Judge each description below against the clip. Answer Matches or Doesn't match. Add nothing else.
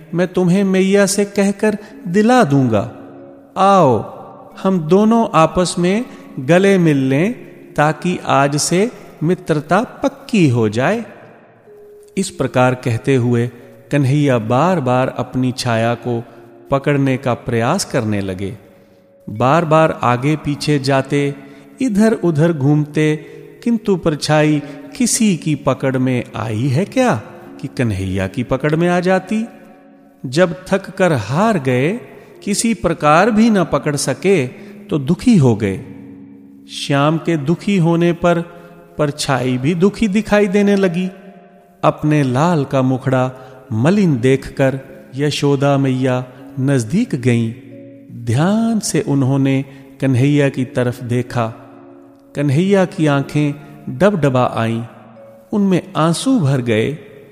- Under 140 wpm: Matches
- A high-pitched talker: Doesn't match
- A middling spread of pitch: Doesn't match